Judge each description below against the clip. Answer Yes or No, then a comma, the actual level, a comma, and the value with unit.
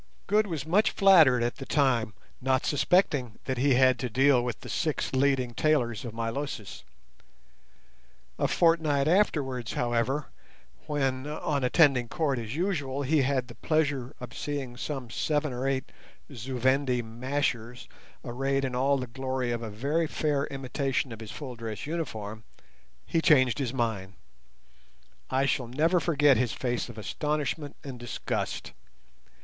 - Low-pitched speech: Yes, low, 130 Hz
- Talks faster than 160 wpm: No, average, 150 wpm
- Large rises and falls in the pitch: No, average, 3.3 semitones